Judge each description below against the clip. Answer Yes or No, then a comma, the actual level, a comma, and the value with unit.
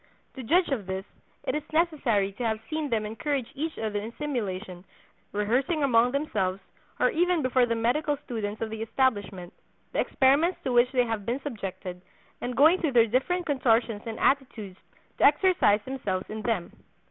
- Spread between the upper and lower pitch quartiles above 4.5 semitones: Yes, average, 5.2 semitones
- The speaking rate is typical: Yes, average, 170 wpm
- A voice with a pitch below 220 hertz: No, high, 240 Hz